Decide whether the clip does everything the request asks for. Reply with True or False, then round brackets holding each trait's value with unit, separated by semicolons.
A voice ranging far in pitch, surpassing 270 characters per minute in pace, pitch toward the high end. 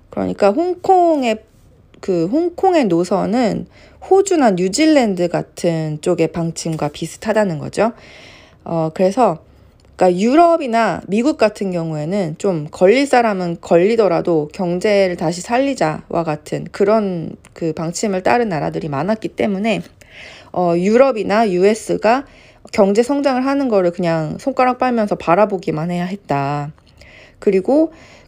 True (5.9 semitones; 280 characters per minute; 200 Hz)